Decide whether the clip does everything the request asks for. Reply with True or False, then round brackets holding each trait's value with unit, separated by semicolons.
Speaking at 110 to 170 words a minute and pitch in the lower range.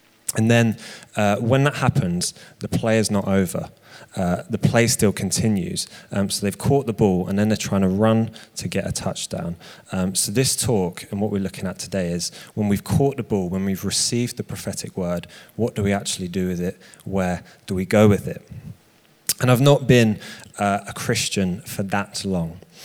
False (200 wpm; 105 Hz)